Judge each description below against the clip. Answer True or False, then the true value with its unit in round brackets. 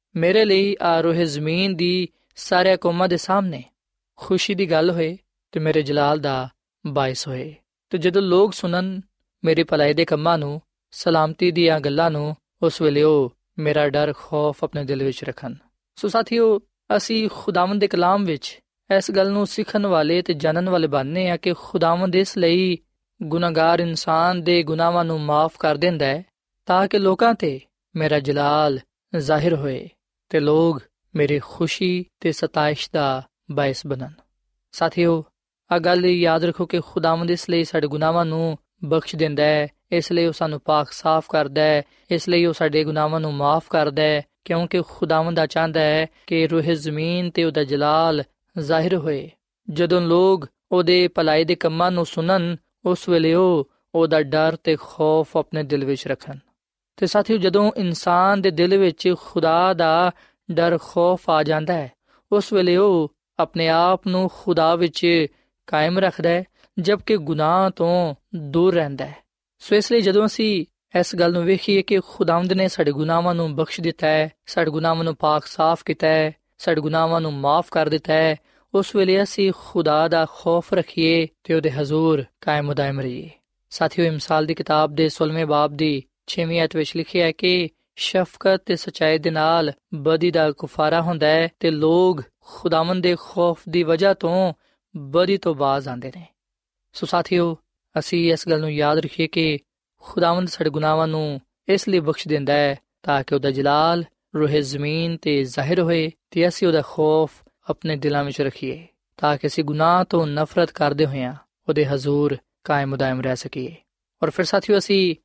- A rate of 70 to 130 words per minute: False (160 wpm)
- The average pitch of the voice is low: False (165 Hz)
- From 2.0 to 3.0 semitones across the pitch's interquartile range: True (2.7 semitones)